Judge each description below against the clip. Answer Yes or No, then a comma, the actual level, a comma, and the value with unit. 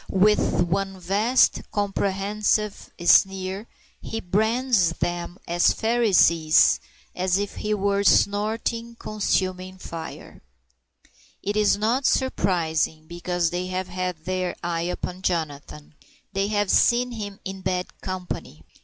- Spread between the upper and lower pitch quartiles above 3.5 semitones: No, average, 3.0 semitones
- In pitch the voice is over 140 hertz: Yes, high, 190 Hz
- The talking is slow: Yes, slow, 115 wpm